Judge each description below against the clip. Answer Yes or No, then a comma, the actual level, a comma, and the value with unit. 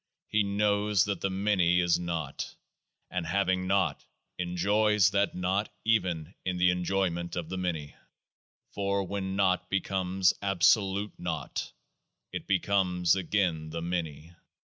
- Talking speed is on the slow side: Yes, slow, 130 wpm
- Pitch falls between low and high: No, very low, 95 Hz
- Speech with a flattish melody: Yes, narrow, 2.3 semitones